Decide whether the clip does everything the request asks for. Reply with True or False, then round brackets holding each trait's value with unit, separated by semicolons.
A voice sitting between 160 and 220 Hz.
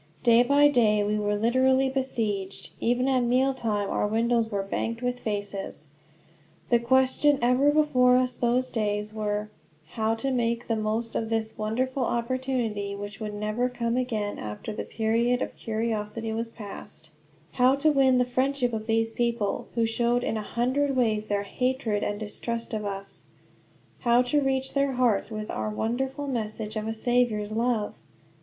False (230 Hz)